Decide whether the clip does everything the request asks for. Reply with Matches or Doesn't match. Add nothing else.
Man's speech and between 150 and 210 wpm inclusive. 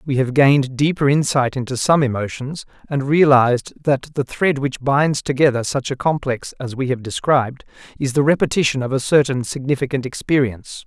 Matches